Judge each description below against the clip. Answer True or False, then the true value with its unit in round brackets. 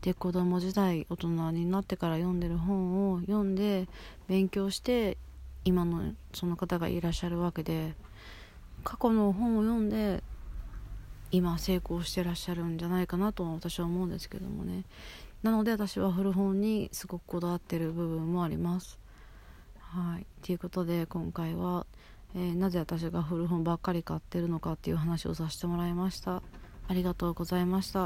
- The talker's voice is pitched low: False (175 Hz)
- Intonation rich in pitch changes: False (2.0 semitones)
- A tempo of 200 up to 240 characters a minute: False (340 characters per minute)